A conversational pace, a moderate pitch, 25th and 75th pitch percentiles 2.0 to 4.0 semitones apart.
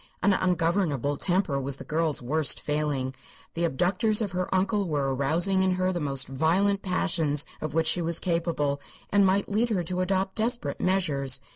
No: average, 175 wpm; medium, 170 Hz; average, 4.6 semitones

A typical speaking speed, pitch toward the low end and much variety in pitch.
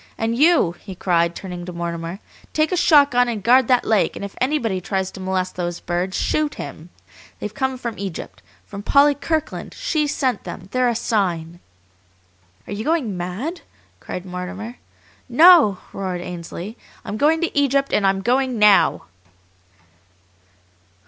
No: average, 155 wpm; high, 210 Hz; wide, 6.7 semitones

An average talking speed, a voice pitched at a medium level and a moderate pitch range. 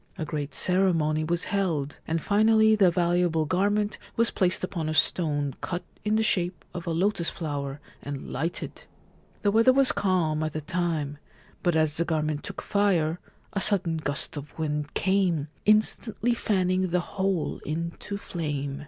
Yes: average, 160 wpm; medium, 170 Hz; average, 4.1 semitones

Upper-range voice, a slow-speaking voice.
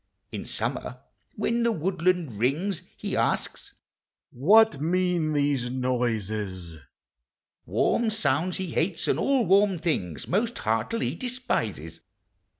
No: medium, 165 Hz; slow, 120 wpm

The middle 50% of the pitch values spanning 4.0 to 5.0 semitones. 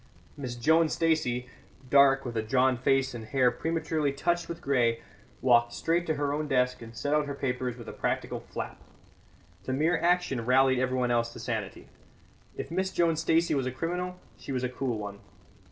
Yes: average, 4.5 semitones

